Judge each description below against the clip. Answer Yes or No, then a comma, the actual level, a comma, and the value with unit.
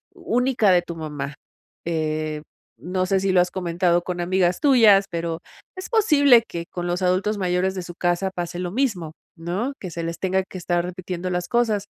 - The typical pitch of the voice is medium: Yes, medium, 180 Hz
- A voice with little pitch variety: Yes, narrow, 2.3 semitones